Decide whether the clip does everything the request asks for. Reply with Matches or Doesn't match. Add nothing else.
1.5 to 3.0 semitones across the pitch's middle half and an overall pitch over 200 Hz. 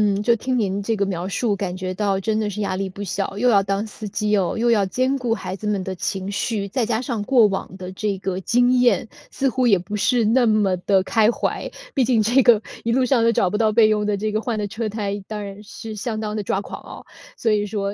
Matches